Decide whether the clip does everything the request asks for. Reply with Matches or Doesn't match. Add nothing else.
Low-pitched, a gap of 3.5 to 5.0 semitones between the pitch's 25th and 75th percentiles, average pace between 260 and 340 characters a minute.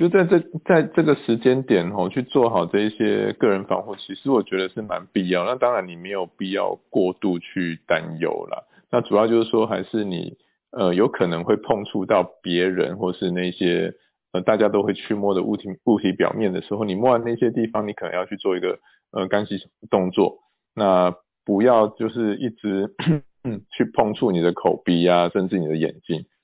Matches